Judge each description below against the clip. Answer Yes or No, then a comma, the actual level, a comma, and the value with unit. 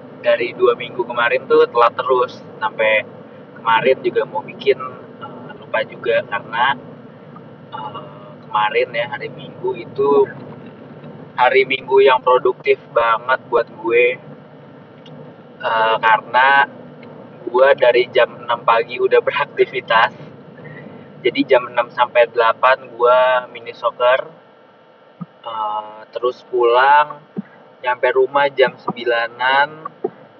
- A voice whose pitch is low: Yes, low, 130 Hz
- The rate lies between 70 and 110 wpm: Yes, average, 105 wpm